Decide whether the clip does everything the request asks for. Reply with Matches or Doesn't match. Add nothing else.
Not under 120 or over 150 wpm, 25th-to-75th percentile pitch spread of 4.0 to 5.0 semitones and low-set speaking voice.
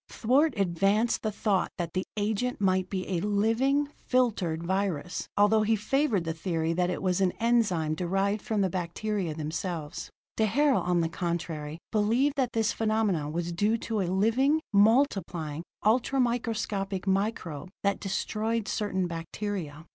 Doesn't match